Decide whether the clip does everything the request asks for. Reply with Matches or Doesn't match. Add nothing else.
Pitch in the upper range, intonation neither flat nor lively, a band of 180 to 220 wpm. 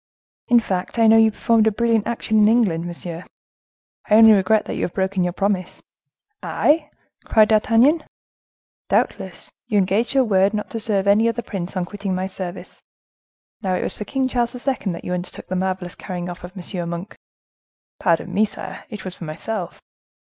Matches